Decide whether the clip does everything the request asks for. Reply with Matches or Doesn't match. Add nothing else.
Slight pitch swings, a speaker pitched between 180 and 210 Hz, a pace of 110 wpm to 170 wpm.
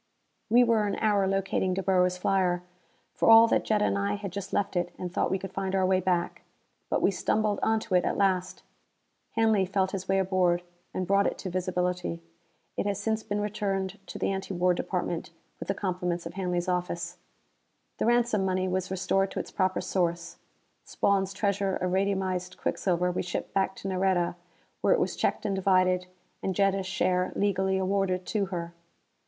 Doesn't match